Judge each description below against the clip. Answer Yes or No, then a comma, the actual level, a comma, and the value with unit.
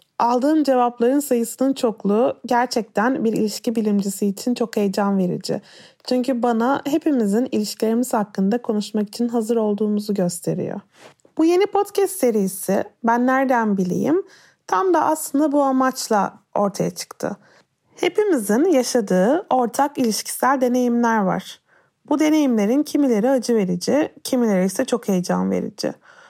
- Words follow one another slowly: No, average, 120 wpm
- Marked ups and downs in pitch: No, average, 4.3 semitones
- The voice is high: Yes, high, 240 Hz